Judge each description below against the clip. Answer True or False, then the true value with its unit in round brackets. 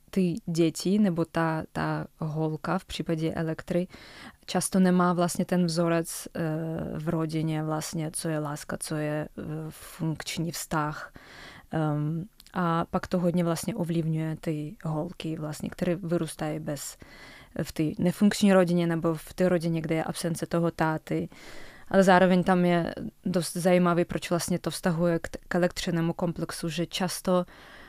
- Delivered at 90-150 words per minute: True (140 wpm)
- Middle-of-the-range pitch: True (170 Hz)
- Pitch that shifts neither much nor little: False (2.1 semitones)